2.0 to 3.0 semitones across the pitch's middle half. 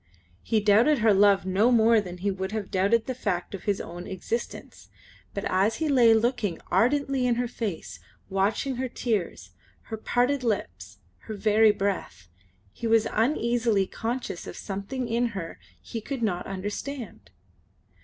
No: average, 3.8 semitones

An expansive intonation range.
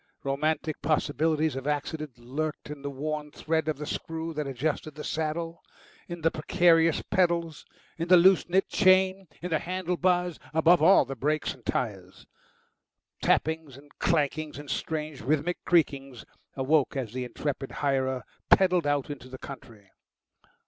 No: average, 3.2 semitones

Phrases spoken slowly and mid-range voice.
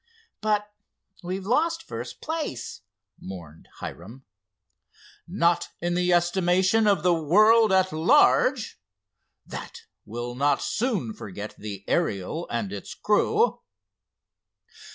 Yes: slow, 105 wpm; medium, 175 Hz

